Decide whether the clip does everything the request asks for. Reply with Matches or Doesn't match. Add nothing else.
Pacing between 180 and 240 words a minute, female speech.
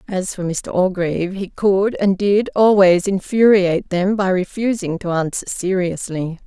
Doesn't match